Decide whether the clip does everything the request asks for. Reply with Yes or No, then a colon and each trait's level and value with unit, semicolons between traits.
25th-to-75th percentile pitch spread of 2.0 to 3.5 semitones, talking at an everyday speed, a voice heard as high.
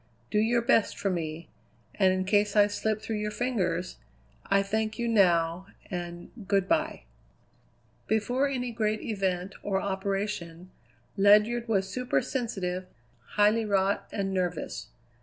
No: average, 2.8 semitones; slow, 130 wpm; high, 200 Hz